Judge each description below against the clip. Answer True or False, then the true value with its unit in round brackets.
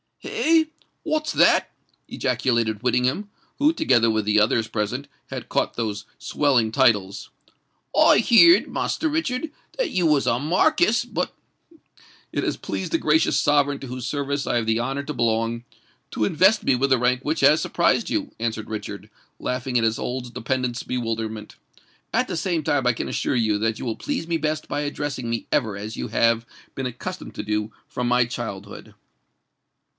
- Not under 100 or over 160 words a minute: False (175 wpm)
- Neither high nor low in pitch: False (125 Hz)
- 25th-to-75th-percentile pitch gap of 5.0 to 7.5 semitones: True (5.4 semitones)